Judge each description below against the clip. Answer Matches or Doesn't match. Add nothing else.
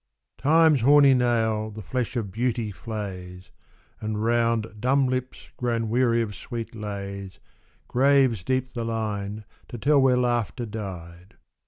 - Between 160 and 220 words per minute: Doesn't match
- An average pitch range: Matches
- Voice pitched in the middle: Doesn't match